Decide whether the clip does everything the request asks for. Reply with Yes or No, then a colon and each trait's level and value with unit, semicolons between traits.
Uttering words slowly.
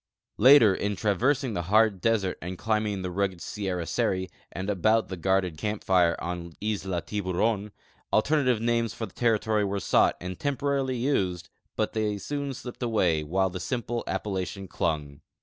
No: average, 165 wpm